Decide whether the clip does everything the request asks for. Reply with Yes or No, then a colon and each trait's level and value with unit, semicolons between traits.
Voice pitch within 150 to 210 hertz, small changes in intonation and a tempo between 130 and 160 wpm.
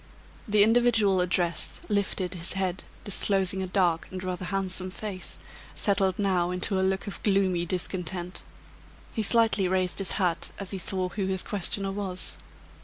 Yes: high, 190 Hz; narrow, 1.6 semitones; average, 155 wpm